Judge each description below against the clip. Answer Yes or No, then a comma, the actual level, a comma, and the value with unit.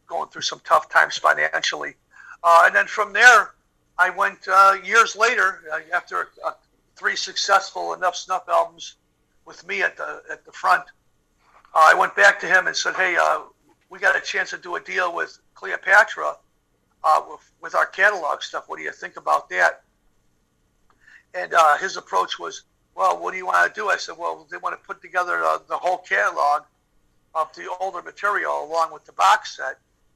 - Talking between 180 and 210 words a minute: Yes, average, 190 wpm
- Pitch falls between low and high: Yes, medium, 180 Hz